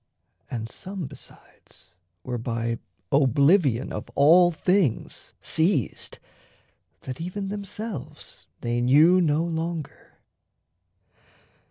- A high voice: No, medium, 155 Hz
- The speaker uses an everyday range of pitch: No, wide, 6.1 semitones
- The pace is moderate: No, slow, 85 wpm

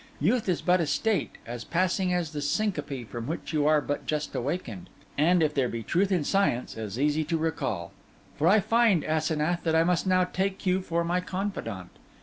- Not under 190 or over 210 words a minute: Yes, average, 200 wpm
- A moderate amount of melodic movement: Yes, average, 4.0 semitones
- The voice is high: No, medium, 165 Hz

